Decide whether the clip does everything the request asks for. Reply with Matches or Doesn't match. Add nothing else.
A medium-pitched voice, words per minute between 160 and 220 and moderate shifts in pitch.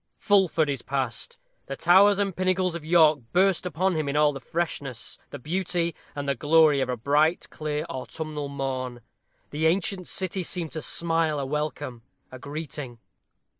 Matches